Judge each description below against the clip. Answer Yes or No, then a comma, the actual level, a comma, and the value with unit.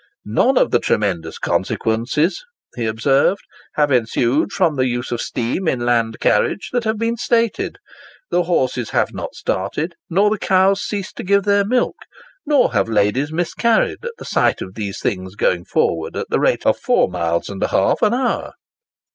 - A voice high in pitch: No, medium, 140 Hz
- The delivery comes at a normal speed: Yes, average, 180 wpm